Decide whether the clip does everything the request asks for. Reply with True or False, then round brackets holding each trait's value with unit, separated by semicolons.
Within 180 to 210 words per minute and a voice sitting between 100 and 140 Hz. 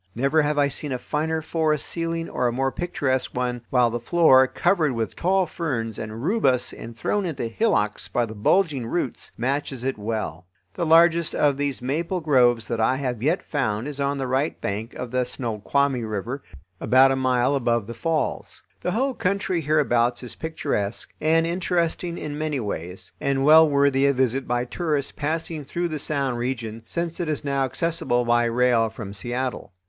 True (185 wpm; 135 Hz)